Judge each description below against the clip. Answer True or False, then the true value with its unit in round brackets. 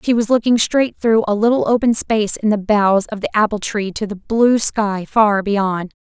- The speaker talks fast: True (220 wpm)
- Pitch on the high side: True (215 Hz)